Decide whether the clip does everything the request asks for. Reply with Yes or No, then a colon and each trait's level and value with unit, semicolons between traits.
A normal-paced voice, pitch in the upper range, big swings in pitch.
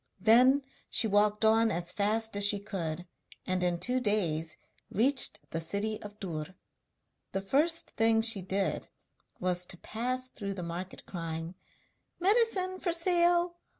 Yes: average, 145 wpm; high, 210 Hz; wide, 5.8 semitones